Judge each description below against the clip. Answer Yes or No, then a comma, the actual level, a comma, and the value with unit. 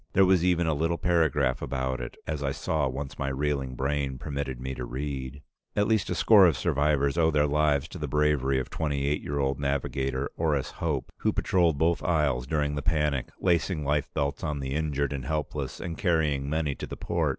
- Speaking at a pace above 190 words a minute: Yes, fast, 205 wpm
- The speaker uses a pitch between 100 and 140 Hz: No, very low, 75 Hz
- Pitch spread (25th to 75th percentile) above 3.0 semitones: No, average, 2.7 semitones